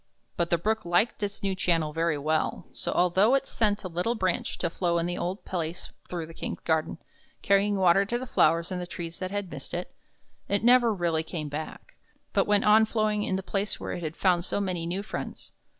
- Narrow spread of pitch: No, average, 3.3 semitones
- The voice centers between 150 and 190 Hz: Yes, medium, 185 Hz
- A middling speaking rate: No, fast, 215 wpm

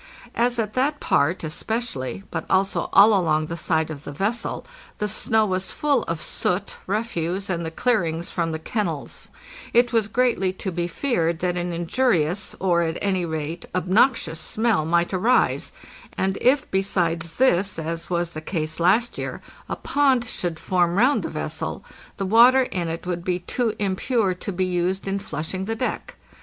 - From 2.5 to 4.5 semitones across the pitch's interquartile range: No, average, 4.9 semitones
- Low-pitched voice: No, medium, 185 Hz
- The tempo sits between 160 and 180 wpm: Yes, average, 175 wpm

